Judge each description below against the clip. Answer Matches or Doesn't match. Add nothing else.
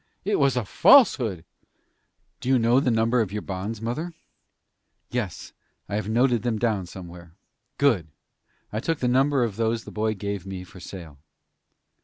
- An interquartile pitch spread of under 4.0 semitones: Doesn't match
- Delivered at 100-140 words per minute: Doesn't match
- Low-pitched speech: Matches